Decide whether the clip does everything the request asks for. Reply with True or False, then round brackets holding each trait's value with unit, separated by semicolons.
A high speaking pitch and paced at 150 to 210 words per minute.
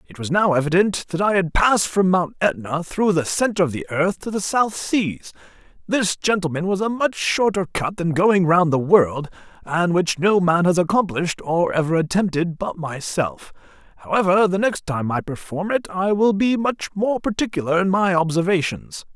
False (180 Hz; 190 wpm)